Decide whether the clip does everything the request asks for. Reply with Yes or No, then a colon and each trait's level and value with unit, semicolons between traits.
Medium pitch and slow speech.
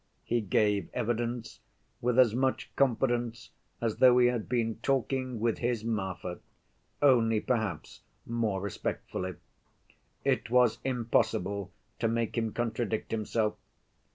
No: low, 115 Hz; slow, 120 wpm